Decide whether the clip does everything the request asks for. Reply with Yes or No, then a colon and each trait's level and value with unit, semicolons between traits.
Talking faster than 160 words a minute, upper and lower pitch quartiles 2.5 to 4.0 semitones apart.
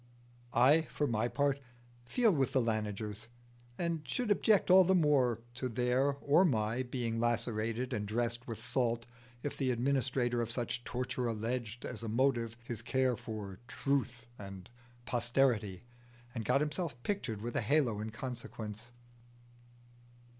No: average, 145 wpm; average, 3.2 semitones